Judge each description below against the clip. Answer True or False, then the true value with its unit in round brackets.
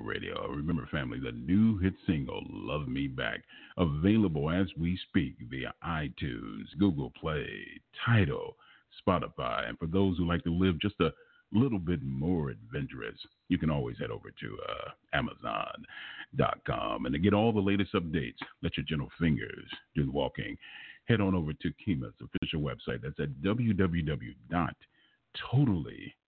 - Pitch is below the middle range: True (95 Hz)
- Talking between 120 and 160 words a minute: True (150 wpm)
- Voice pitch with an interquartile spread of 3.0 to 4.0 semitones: True (3.4 semitones)